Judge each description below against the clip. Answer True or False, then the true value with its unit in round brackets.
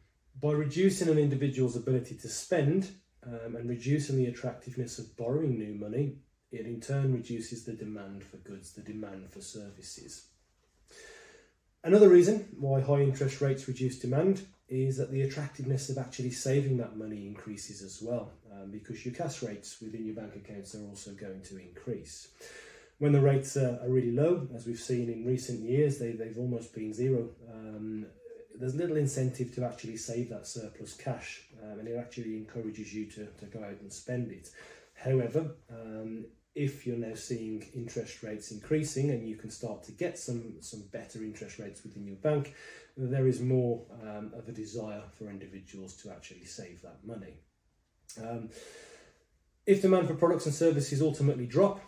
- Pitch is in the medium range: False (120 Hz)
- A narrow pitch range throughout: False (4.3 semitones)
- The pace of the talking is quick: False (170 wpm)